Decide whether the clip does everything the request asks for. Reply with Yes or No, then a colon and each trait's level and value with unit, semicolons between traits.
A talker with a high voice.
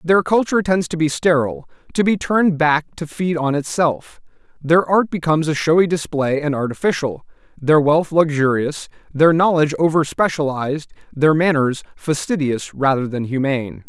No: medium, 155 Hz